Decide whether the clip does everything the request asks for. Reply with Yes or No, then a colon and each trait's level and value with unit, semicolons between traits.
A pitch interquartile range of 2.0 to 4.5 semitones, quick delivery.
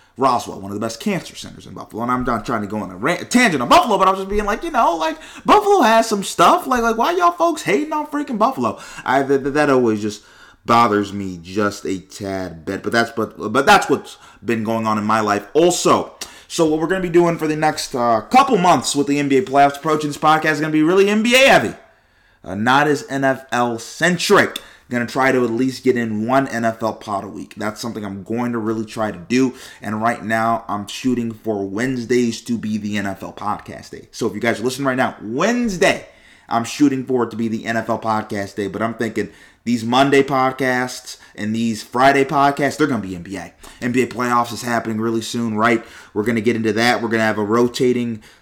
No: average, 4.9 semitones; fast, 235 wpm